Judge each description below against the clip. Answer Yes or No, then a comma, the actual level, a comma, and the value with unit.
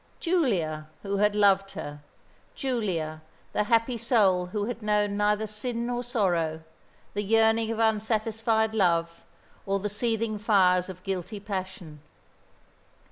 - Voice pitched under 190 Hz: No, high, 210 Hz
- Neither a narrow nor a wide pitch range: Yes, average, 3.3 semitones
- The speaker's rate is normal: No, slow, 130 wpm